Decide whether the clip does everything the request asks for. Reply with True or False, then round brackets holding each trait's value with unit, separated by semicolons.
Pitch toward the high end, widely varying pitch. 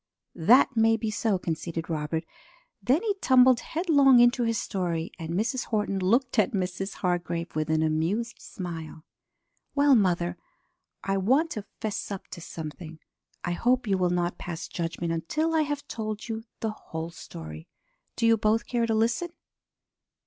True (200 Hz; 6.0 semitones)